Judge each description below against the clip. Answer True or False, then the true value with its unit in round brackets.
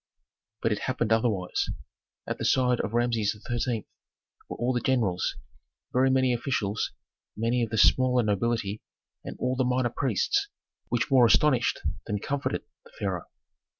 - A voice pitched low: True (120 Hz)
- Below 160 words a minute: True (150 wpm)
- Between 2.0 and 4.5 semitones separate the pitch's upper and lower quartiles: True (2.6 semitones)